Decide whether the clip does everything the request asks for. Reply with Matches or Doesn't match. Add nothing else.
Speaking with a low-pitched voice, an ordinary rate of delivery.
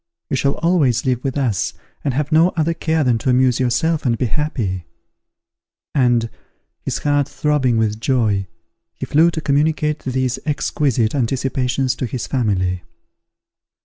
Matches